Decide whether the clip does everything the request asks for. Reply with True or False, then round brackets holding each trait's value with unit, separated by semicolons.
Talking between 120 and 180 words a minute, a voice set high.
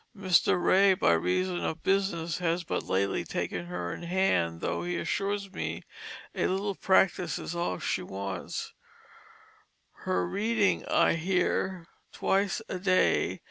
False (140 wpm; 180 Hz)